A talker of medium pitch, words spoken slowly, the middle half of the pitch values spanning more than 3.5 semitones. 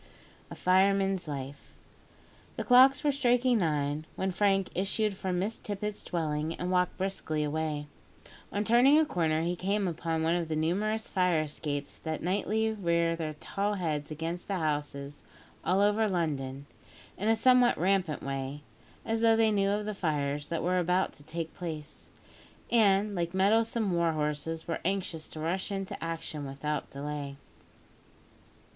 No: medium, 175 Hz; average, 155 wpm; average, 4.6 semitones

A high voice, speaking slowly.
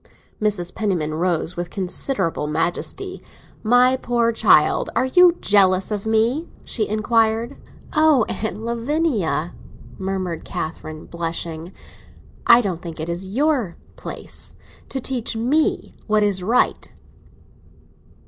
Yes: high, 210 Hz; slow, 115 wpm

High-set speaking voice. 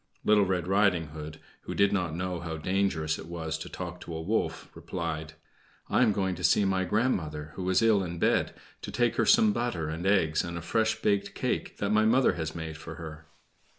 No: very low, 90 Hz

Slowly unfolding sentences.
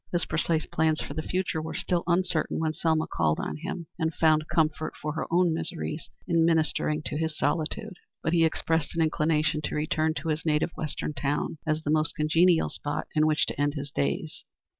No: average, 200 wpm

